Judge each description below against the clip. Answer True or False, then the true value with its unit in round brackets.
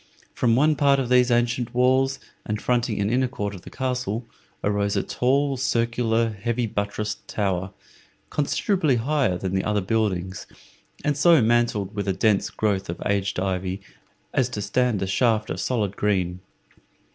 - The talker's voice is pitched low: True (115 Hz)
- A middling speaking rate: True (160 wpm)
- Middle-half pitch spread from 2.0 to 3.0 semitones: False (3.9 semitones)